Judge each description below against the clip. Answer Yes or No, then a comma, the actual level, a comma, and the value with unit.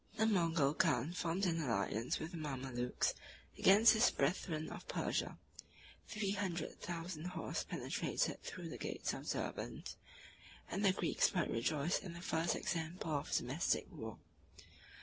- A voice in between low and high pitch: Yes, medium, 165 Hz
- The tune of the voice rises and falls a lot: No, average, 4.3 semitones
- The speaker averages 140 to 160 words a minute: Yes, average, 145 wpm